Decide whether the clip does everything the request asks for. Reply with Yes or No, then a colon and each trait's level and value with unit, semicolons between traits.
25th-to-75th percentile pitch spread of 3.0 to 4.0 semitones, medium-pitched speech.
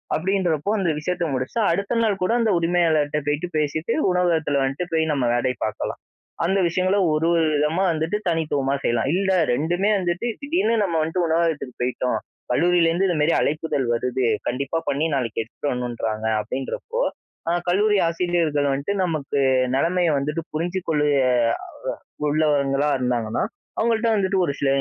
No: average, 4.5 semitones; medium, 160 Hz